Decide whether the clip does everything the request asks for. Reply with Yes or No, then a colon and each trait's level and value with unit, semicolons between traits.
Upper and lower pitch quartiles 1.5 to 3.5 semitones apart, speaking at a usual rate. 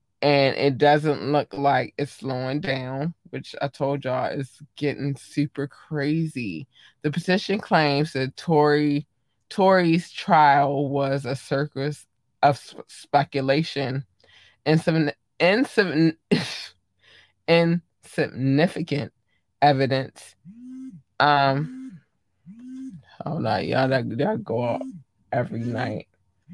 No: average, 3.0 semitones; slow, 95 wpm